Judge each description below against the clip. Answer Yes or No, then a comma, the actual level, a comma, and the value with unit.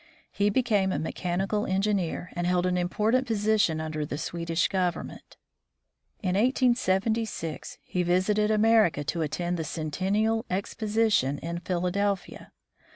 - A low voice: No, high, 190 Hz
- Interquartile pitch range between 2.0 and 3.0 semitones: No, average, 3.6 semitones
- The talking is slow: Yes, slow, 120 wpm